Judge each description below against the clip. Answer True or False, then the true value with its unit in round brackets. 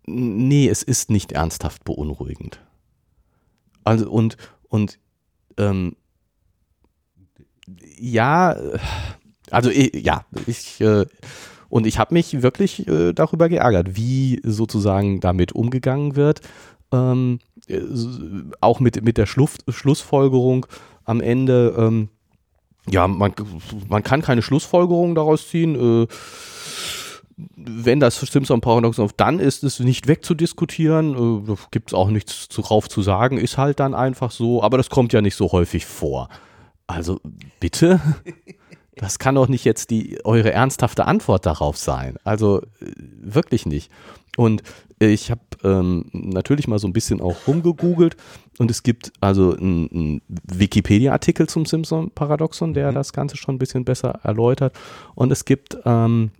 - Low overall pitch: True (115 Hz)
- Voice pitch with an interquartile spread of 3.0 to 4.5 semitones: False (5.1 semitones)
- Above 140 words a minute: False (135 wpm)